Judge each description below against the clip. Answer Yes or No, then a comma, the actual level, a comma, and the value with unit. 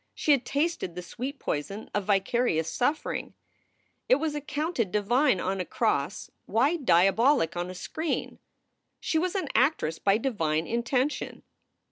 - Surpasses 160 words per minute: No, average, 140 wpm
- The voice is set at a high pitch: Yes, high, 235 Hz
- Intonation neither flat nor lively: No, wide, 7.8 semitones